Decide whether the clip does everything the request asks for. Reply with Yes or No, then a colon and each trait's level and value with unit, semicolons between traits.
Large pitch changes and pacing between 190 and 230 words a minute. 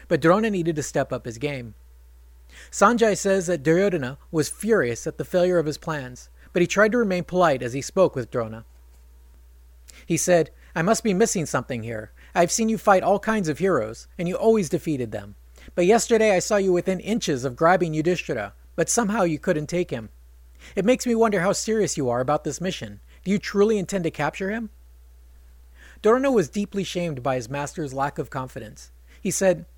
Yes: wide, 8.8 semitones; average, 200 wpm